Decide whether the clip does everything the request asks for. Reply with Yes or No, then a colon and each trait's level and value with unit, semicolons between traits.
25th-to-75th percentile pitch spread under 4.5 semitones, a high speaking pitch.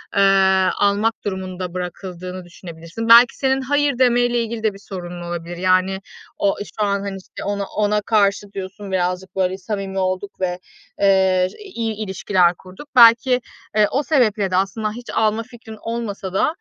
Yes: average, 3.4 semitones; high, 195 Hz